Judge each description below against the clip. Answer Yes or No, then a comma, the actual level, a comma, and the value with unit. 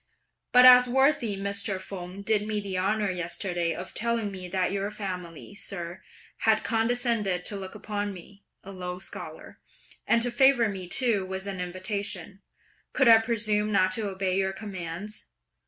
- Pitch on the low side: No, high, 200 Hz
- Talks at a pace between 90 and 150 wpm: No, average, 160 wpm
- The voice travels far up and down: No, average, 2.8 semitones